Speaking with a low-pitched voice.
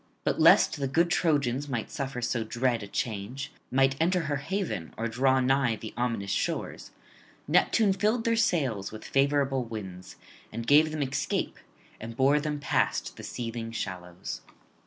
Yes: low, 130 Hz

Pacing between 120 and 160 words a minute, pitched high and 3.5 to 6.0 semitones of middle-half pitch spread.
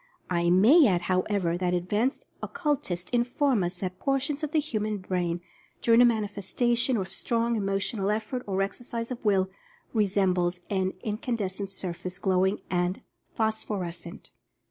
Yes: average, 150 wpm; high, 200 Hz; average, 4.2 semitones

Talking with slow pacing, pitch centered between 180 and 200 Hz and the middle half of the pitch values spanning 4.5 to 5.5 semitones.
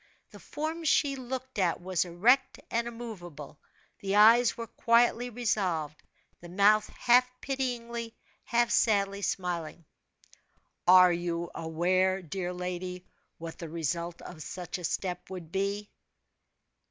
Yes: slow, 125 wpm; high, 190 Hz; average, 5.2 semitones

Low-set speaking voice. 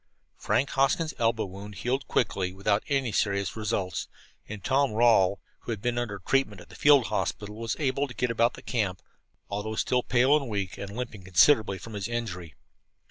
Yes: low, 110 Hz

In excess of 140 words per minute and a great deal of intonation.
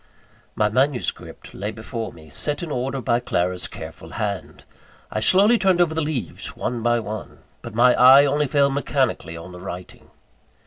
Yes: average, 175 wpm; wide, 5.9 semitones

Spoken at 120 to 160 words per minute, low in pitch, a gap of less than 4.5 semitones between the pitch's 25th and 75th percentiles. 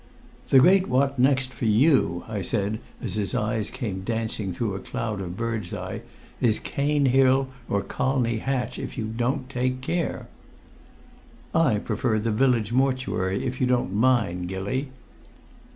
Yes: average, 150 wpm; low, 120 Hz; average, 3.8 semitones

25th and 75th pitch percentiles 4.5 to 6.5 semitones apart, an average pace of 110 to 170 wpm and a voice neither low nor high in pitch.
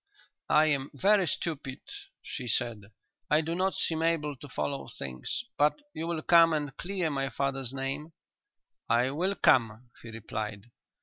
Yes: average, 4.8 semitones; average, 150 wpm; medium, 145 Hz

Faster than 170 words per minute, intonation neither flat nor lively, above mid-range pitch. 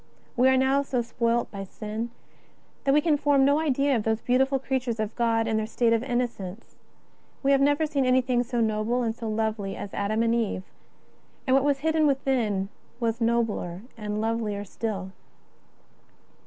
Yes: average, 180 wpm; average, 3.5 semitones; high, 235 Hz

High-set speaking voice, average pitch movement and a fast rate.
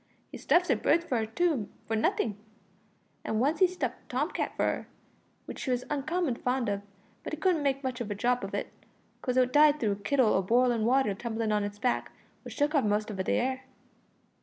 Yes: very high, 250 Hz; average, 4.7 semitones; fast, 225 wpm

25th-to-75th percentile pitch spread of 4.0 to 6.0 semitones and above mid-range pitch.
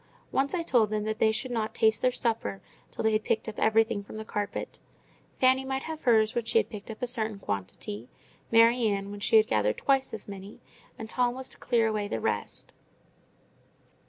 No: average, 2.7 semitones; high, 220 Hz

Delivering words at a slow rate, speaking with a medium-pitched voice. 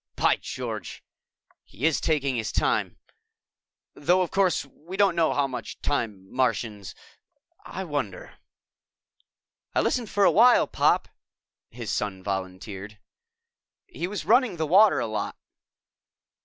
Yes: slow, 130 wpm; medium, 145 Hz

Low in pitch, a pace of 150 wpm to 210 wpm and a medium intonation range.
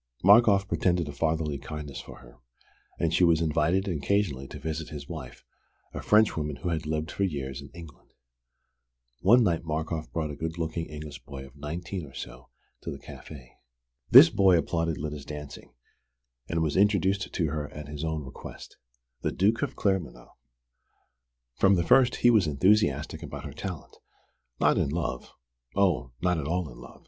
Yes: very low, 80 Hz; average, 170 wpm; average, 3.9 semitones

